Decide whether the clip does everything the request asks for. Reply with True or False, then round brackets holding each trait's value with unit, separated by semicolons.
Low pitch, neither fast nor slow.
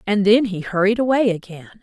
False (205 Hz; 195 wpm)